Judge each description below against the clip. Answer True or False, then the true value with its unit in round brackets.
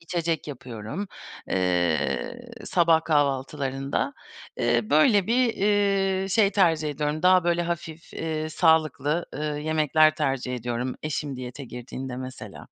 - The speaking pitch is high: False (155 Hz)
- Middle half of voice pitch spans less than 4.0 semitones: False (4.6 semitones)